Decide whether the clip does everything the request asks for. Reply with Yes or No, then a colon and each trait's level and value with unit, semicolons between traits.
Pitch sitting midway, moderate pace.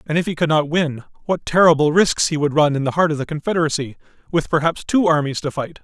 No: medium, 155 Hz; fast, 245 wpm